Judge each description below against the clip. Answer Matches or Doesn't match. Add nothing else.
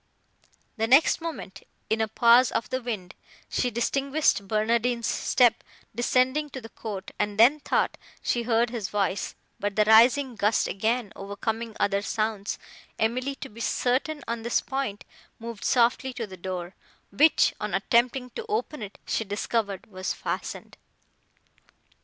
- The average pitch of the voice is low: Doesn't match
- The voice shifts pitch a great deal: Doesn't match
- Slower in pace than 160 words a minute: Matches